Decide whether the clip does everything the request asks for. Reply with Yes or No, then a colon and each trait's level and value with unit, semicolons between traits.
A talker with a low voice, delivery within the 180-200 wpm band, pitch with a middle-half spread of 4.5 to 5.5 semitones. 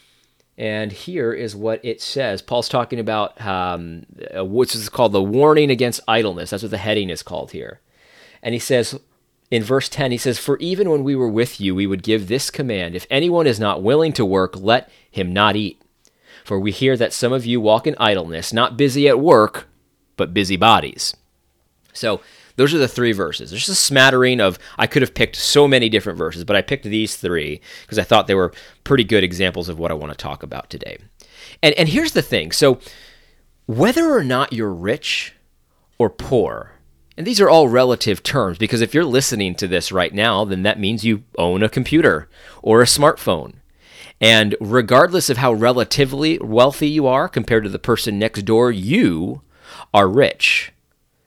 Yes: low, 110 Hz; average, 195 wpm; average, 4.8 semitones